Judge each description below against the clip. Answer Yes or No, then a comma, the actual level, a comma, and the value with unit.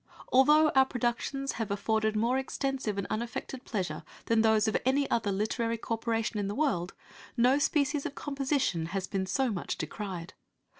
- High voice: Yes, high, 230 Hz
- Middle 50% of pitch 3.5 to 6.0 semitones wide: Yes, average, 4.5 semitones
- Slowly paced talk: No, average, 160 wpm